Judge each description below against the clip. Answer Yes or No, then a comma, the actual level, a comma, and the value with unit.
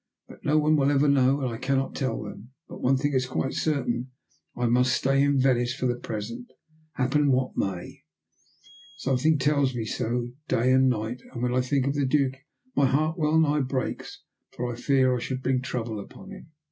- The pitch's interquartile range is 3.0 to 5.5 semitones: No, narrow, 2.4 semitones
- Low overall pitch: Yes, low, 130 Hz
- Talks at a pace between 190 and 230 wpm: Yes, average, 195 wpm